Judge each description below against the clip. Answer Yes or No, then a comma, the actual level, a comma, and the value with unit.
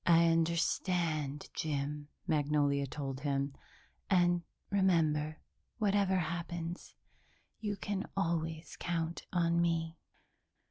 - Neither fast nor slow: No, slow, 90 wpm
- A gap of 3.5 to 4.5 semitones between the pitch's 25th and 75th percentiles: No, average, 2.7 semitones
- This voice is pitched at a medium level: Yes, medium, 165 Hz